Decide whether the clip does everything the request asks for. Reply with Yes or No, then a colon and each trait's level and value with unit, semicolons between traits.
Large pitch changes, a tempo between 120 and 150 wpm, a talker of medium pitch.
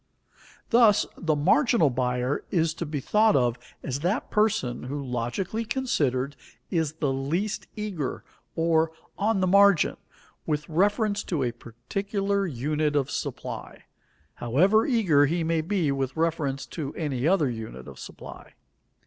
Yes: wide, 6.6 semitones; average, 140 wpm; medium, 160 Hz